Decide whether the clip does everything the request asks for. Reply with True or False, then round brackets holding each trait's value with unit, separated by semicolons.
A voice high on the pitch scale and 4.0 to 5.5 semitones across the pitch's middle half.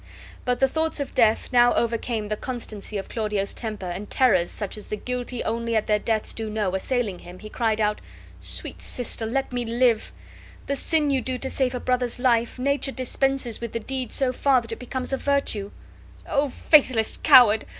False (240 Hz; 3.2 semitones)